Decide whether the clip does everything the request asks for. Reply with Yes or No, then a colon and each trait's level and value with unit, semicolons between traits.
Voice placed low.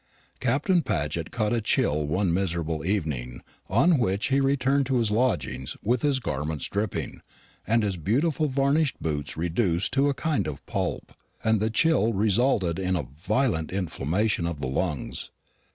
Yes: low, 100 Hz